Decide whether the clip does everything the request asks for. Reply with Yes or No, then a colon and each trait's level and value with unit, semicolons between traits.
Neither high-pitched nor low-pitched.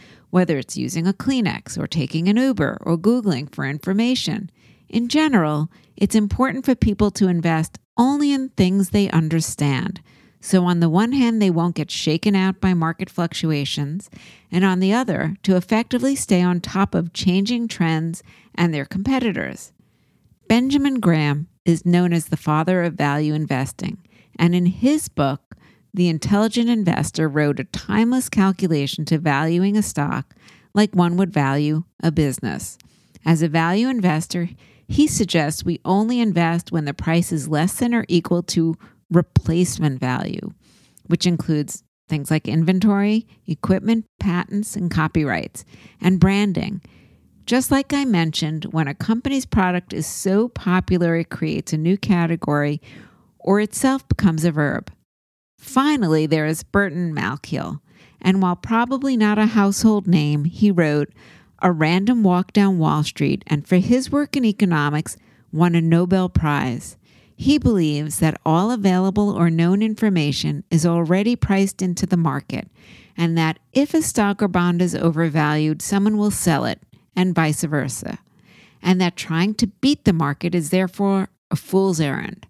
Yes: medium, 180 Hz